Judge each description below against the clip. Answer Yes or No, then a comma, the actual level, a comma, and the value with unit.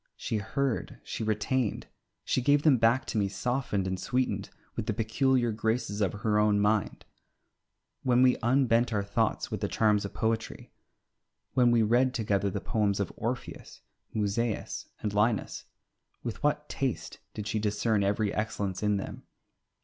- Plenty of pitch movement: No, average, 3.0 semitones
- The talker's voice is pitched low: Yes, low, 110 Hz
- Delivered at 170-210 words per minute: No, average, 155 wpm